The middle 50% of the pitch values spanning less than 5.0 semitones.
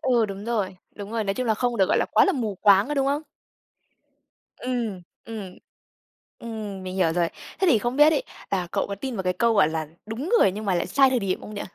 Yes: average, 4.2 semitones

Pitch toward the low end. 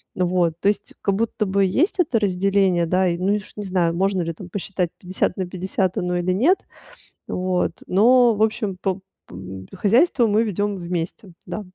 No: high, 190 Hz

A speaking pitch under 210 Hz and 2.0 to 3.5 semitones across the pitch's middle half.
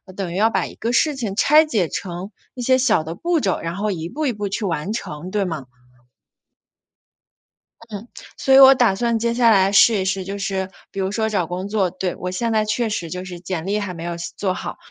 No: high, 200 Hz; average, 3.9 semitones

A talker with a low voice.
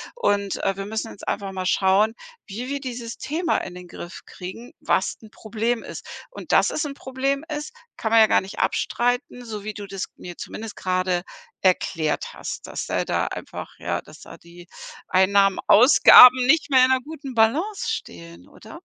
No: high, 220 Hz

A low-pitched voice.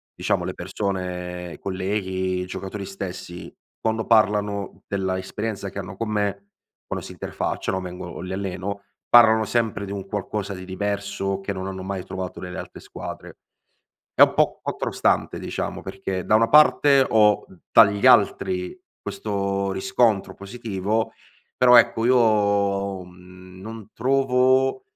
Yes: low, 100 Hz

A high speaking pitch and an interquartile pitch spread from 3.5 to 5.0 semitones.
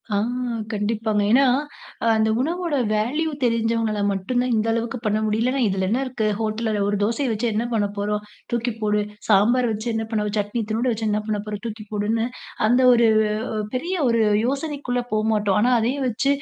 No: high, 225 Hz; narrow, 2.6 semitones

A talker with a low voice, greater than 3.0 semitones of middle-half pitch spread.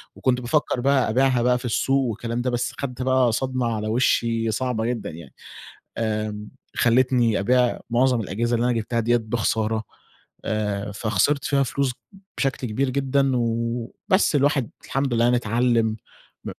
No: low, 120 Hz; narrow, 2.5 semitones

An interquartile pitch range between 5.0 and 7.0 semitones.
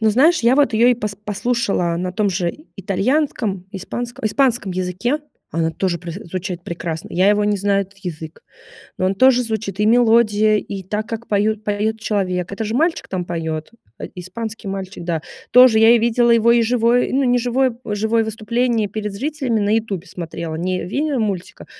No: average, 4.0 semitones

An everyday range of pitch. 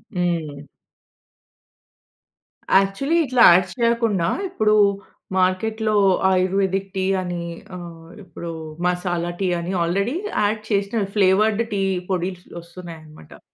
Yes: average, 3.2 semitones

